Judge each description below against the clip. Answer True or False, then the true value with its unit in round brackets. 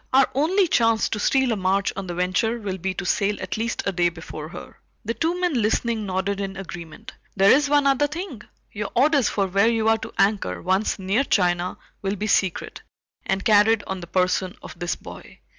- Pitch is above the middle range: True (205 Hz)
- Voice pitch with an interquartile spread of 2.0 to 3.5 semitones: False (3.9 semitones)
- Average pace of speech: False (210 wpm)